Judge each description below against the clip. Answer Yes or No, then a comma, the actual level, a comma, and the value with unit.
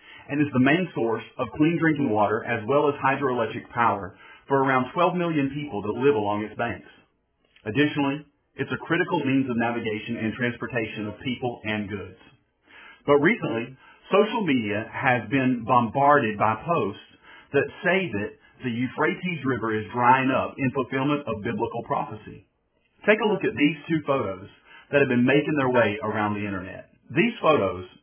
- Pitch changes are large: No, average, 4.5 semitones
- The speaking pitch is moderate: No, low, 130 Hz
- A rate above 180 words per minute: No, average, 165 wpm